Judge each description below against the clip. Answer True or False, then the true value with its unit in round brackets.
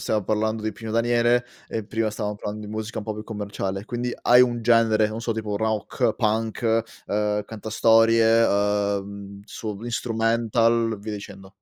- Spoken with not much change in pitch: True (1.7 semitones)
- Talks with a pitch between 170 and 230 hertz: False (110 Hz)